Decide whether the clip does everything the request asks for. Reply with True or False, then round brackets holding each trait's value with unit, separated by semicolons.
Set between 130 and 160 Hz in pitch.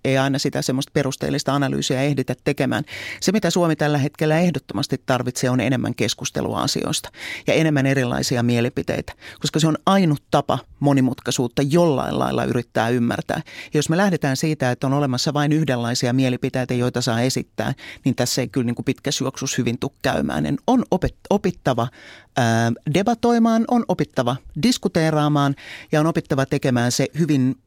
True (135 Hz)